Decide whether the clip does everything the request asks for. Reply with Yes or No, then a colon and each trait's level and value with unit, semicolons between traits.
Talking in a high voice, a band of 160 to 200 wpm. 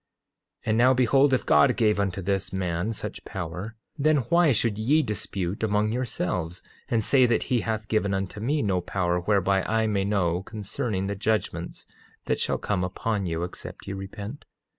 No: low, 105 Hz; average, 180 wpm